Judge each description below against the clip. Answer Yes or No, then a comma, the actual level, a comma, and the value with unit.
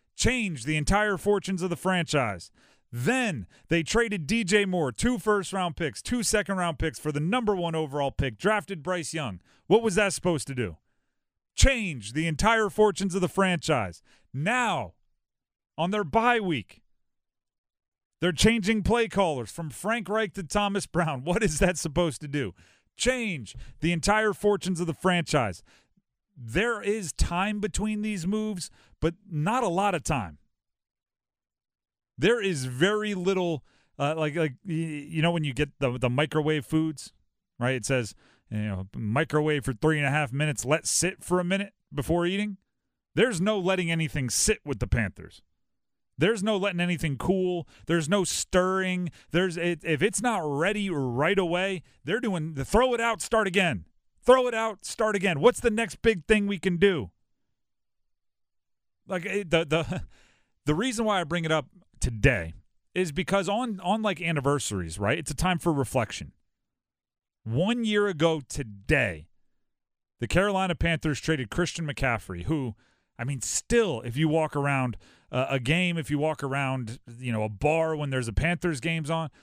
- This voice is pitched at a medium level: Yes, medium, 165 Hz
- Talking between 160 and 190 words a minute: Yes, average, 165 wpm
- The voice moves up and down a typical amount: No, wide, 6.6 semitones